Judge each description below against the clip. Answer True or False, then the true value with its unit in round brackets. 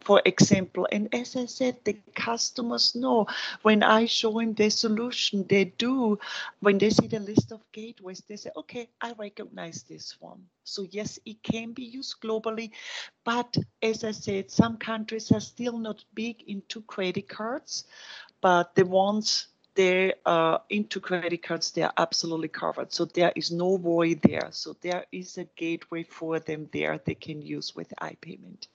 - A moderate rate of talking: True (175 wpm)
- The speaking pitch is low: False (210 Hz)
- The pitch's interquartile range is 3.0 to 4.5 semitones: True (3.8 semitones)